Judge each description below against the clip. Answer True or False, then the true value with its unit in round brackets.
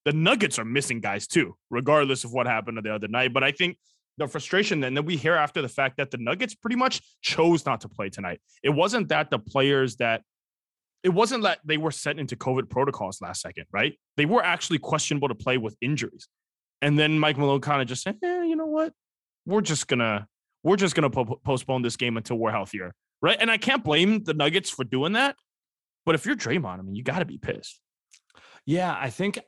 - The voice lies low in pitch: False (145 Hz)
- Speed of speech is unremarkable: False (220 wpm)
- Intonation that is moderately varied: False (5.9 semitones)